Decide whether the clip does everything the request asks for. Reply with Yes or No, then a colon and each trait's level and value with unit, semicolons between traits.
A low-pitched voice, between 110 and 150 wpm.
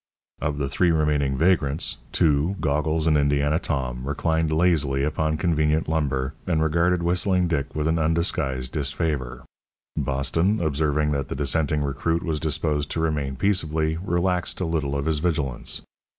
Yes: very low, 75 Hz; average, 145 wpm